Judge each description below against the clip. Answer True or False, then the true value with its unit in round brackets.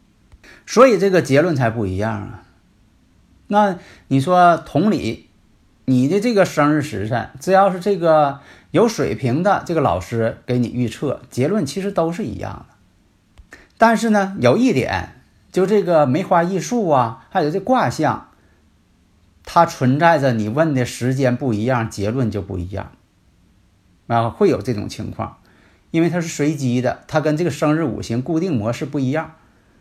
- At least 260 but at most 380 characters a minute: False (235 characters per minute)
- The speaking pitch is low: True (125 Hz)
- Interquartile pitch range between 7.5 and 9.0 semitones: True (7.8 semitones)